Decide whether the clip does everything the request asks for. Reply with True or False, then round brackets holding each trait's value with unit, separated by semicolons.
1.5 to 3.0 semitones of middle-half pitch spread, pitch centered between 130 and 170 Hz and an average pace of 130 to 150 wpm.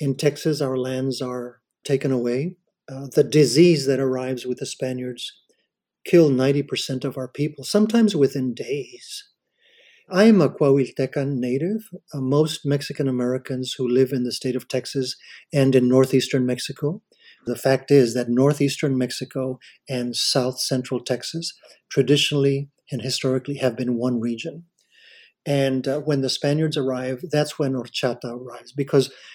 True (2.5 semitones; 135 Hz; 145 wpm)